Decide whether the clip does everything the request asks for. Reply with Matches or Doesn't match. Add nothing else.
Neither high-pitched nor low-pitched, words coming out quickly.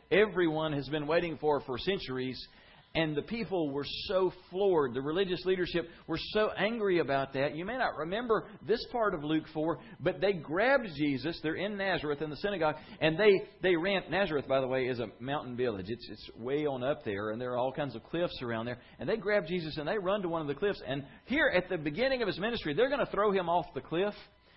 Matches